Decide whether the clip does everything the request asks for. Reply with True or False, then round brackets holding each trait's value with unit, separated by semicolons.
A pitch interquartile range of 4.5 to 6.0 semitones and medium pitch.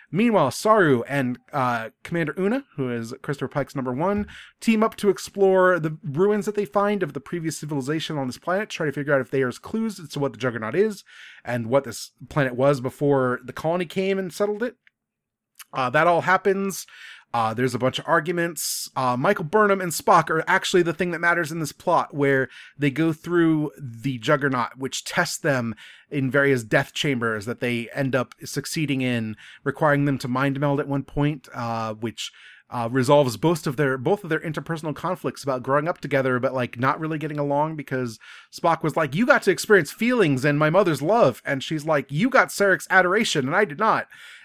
True (4.8 semitones; 150 Hz)